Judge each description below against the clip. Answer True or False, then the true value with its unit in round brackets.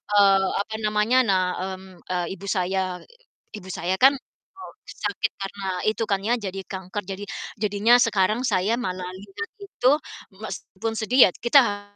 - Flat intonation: False (3.1 semitones)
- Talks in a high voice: True (205 Hz)